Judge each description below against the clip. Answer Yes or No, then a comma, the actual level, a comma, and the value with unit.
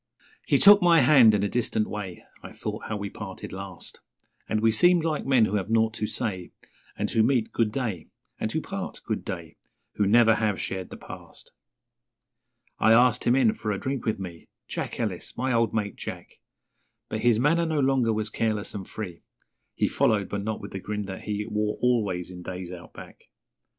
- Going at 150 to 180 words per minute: No, average, 200 wpm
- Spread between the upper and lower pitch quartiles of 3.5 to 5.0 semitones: No, average, 3.1 semitones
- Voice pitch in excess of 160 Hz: No, low, 110 Hz